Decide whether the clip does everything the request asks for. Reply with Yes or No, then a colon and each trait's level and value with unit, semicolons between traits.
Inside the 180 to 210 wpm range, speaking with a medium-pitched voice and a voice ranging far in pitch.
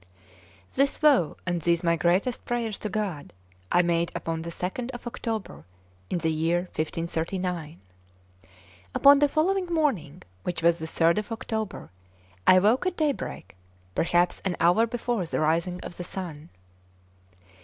No: average, 145 wpm; medium, 180 Hz; wide, 5.9 semitones